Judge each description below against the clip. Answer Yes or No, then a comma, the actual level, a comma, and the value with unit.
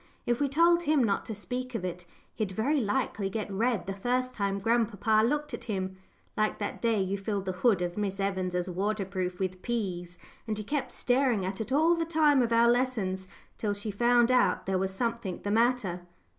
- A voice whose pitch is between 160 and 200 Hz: No, high, 215 Hz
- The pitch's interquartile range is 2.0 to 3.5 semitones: No, average, 4.3 semitones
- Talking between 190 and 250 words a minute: Yes, average, 200 wpm